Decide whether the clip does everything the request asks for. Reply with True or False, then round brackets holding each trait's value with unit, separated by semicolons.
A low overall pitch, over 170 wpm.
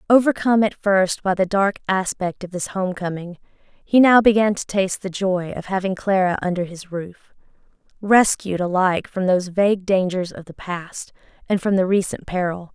False (190 Hz; 180 wpm)